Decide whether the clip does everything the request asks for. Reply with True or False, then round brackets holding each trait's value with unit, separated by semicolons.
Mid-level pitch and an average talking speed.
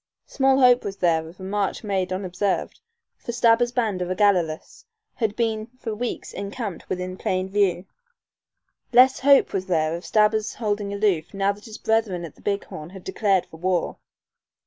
False (200 Hz; 170 wpm)